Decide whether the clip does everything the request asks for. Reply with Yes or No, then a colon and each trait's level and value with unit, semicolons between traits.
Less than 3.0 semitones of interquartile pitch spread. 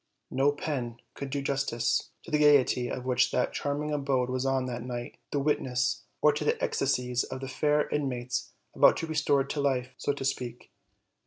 Yes: narrow, 2.4 semitones